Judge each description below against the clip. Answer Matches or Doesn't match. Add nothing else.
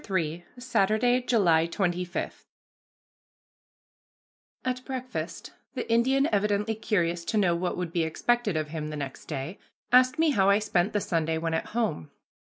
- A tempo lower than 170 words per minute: Matches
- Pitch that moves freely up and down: Matches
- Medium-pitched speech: Doesn't match